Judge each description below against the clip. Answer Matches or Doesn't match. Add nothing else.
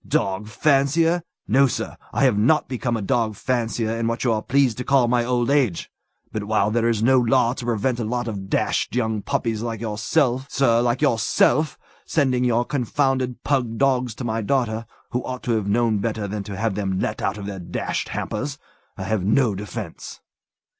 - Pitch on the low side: Matches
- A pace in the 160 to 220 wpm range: Matches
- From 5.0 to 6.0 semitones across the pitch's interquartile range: Doesn't match